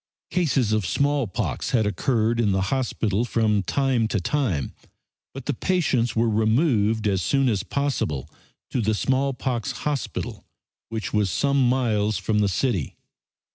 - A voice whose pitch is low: Yes, low, 115 Hz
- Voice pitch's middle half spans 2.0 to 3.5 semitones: No, average, 4.3 semitones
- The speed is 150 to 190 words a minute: No, average, 140 wpm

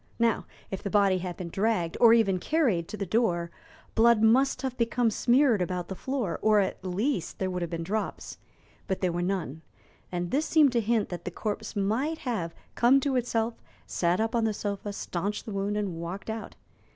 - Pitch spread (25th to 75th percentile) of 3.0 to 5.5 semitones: Yes, average, 4.4 semitones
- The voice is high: Yes, high, 210 Hz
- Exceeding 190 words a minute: Yes, average, 200 wpm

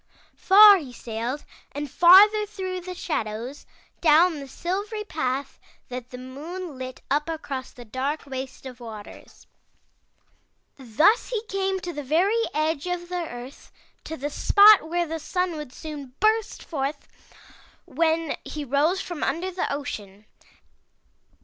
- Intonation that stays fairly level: No, wide, 5.6 semitones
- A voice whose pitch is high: Yes, very high, 310 Hz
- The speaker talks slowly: No, average, 145 wpm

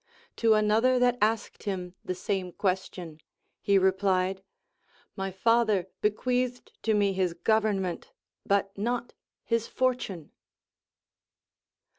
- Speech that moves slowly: Yes, slow, 105 wpm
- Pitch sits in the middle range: No, high, 200 Hz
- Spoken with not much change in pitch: No, average, 3.3 semitones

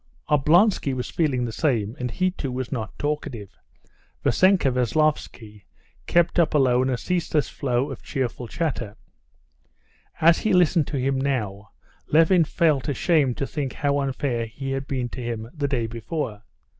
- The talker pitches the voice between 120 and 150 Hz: Yes, low, 135 Hz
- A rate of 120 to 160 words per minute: Yes, average, 155 wpm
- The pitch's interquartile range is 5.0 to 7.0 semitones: No, average, 4.2 semitones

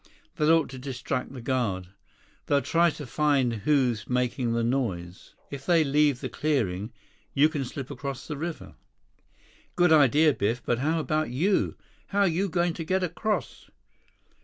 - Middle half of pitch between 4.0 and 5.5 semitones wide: Yes, average, 4.5 semitones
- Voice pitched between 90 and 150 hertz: Yes, medium, 140 Hz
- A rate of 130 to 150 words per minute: No, average, 160 wpm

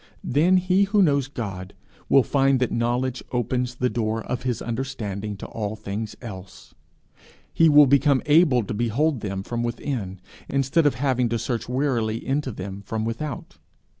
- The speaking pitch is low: Yes, low, 125 Hz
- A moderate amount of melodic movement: Yes, average, 4.1 semitones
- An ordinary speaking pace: Yes, average, 165 wpm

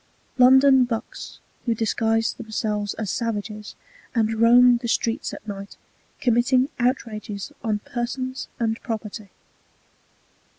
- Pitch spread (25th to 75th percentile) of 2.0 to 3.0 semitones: Yes, narrow, 2.5 semitones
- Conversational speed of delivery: No, slow, 120 wpm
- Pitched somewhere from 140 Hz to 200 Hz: No, high, 230 Hz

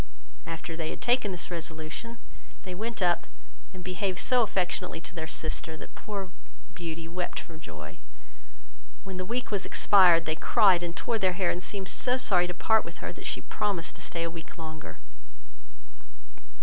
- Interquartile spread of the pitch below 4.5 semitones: Yes, average, 3.2 semitones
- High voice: No, medium, 180 Hz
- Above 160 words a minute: Yes, average, 175 wpm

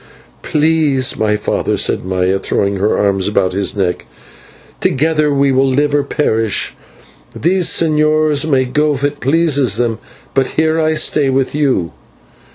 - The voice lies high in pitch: No, low, 135 Hz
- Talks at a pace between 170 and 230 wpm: No, average, 150 wpm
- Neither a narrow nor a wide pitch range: No, wide, 5.9 semitones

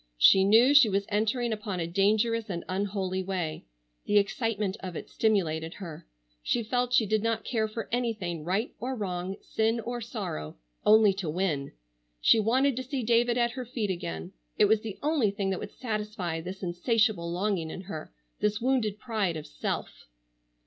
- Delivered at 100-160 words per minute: No, average, 175 wpm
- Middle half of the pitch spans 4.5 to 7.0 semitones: No, average, 3.9 semitones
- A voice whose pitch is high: Yes, high, 210 Hz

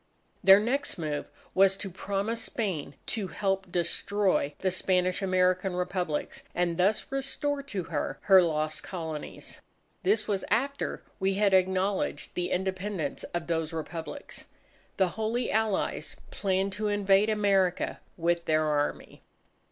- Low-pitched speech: No, high, 190 Hz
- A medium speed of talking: No, slow, 130 wpm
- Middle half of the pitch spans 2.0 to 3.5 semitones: Yes, average, 2.9 semitones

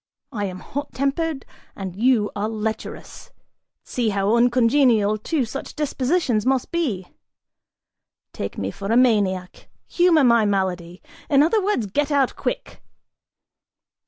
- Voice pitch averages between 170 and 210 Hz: No, high, 235 Hz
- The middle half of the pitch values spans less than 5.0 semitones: No, wide, 5.6 semitones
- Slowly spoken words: Yes, slow, 130 wpm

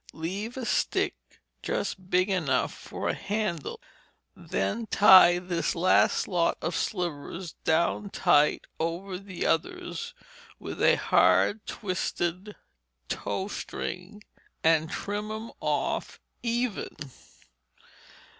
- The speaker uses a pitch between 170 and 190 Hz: Yes, medium, 185 Hz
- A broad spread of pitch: No, average, 3.7 semitones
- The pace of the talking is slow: Yes, slow, 105 wpm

